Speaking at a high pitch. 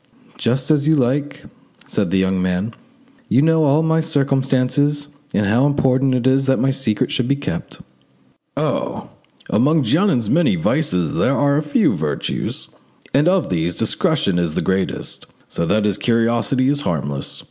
No: low, 130 Hz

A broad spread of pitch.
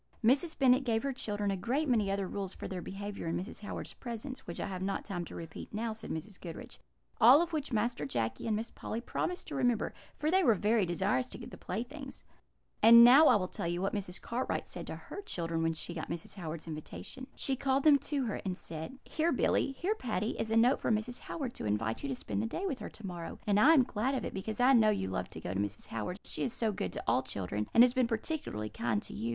Yes: wide, 6.7 semitones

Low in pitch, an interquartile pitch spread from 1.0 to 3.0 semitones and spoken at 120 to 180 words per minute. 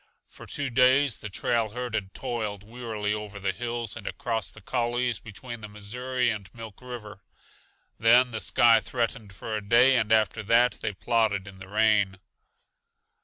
Yes: low, 110 Hz; average, 2.7 semitones; average, 170 wpm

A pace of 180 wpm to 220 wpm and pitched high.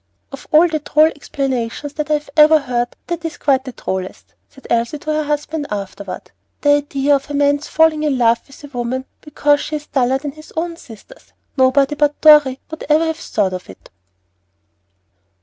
Yes: average, 185 wpm; very high, 290 Hz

